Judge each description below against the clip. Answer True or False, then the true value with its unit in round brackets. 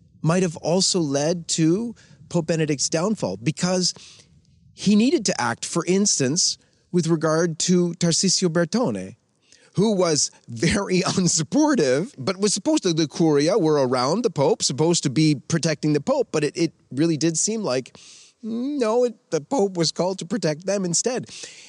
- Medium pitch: True (170 Hz)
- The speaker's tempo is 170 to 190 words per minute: False (160 wpm)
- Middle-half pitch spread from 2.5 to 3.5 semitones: False (4.0 semitones)